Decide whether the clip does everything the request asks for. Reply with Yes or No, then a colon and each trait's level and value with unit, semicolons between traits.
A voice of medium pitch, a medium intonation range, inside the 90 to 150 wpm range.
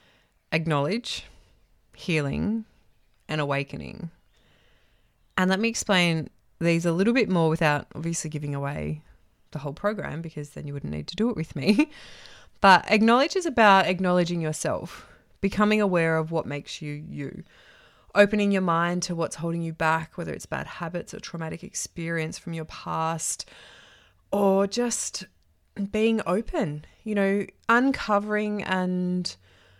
Yes: medium, 170 Hz; average, 5.0 semitones; average, 140 wpm